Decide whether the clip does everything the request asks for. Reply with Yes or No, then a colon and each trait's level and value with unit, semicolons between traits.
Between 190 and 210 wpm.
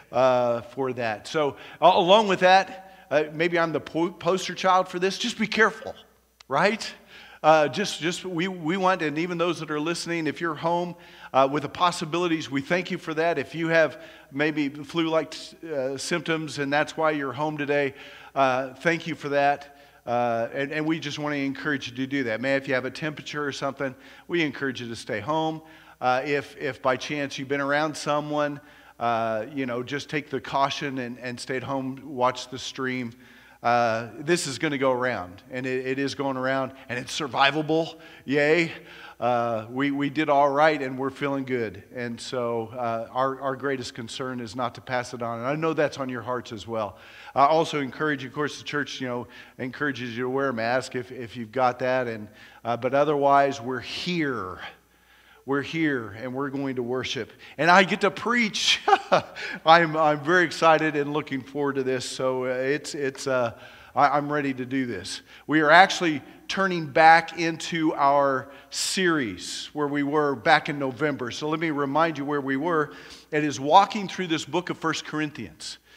Yes: average, 200 wpm